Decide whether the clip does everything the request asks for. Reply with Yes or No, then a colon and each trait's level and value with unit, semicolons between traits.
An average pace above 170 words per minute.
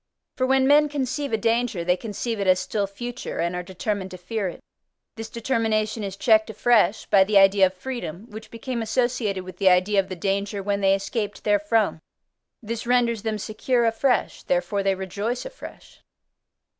Yes: average, 180 wpm